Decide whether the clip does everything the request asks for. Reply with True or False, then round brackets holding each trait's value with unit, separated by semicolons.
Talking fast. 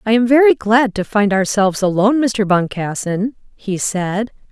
False (160 wpm)